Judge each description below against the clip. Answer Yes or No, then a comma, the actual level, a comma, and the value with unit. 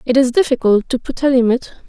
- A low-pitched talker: No, very high, 250 Hz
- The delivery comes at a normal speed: No, fast, 225 wpm